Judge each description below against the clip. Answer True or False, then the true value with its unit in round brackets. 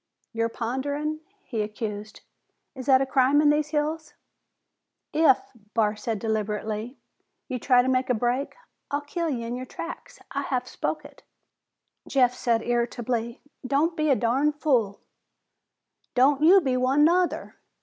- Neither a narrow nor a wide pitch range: True (4.0 semitones)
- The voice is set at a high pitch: True (255 Hz)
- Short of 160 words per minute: True (150 wpm)